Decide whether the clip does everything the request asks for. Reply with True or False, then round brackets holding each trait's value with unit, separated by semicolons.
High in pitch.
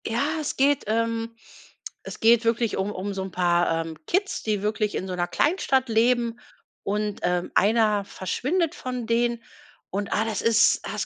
True (225 Hz)